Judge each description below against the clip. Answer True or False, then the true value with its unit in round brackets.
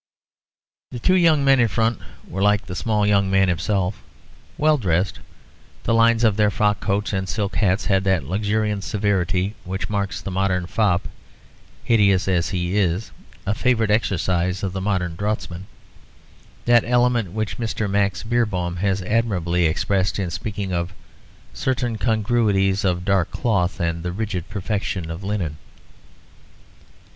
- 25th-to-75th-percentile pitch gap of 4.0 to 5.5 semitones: False (3.0 semitones)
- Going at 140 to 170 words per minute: True (150 wpm)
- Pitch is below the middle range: True (100 Hz)